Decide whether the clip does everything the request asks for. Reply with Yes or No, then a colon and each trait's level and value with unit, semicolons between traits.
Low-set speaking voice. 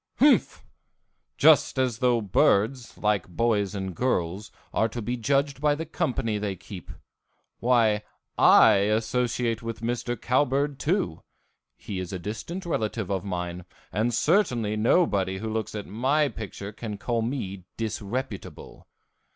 Yes: low, 115 Hz